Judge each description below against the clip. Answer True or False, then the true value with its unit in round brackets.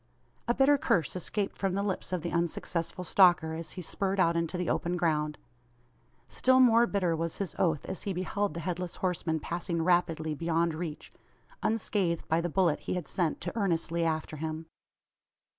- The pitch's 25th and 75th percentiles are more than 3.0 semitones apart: False (2.6 semitones)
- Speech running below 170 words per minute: False (175 wpm)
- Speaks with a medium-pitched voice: True (175 Hz)